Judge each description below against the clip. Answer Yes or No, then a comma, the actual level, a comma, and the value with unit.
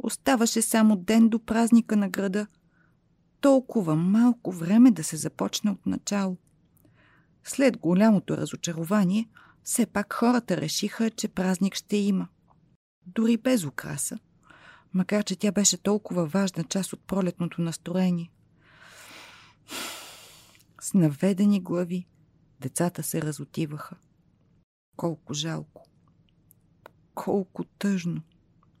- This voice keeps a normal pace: No, slow, 100 wpm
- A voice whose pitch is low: No, high, 190 Hz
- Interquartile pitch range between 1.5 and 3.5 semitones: No, average, 4.4 semitones